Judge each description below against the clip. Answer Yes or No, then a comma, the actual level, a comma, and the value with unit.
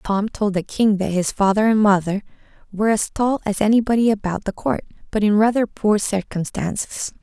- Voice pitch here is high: Yes, high, 205 Hz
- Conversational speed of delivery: Yes, average, 185 wpm